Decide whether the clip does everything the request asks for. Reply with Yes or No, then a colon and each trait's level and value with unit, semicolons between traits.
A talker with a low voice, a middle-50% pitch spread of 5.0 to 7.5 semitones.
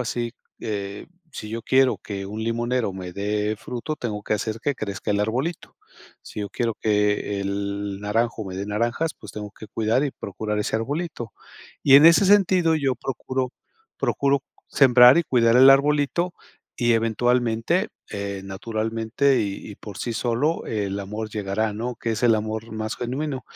No: low, 115 Hz; average, 3.8 semitones